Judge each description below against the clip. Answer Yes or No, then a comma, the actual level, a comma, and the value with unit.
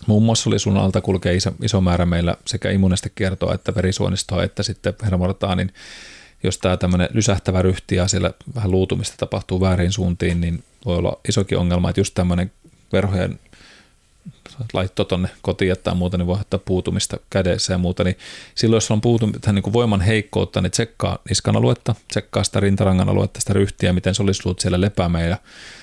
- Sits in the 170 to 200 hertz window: No, very low, 95 Hz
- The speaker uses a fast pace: Yes, fast, 180 wpm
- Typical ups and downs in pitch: No, narrow, 2.3 semitones